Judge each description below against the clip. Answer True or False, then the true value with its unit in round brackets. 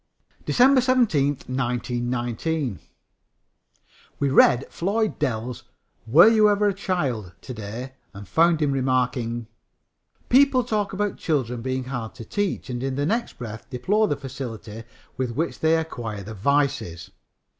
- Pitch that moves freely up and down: True (6.5 semitones)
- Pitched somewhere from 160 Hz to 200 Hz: False (135 Hz)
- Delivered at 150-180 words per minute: False (135 wpm)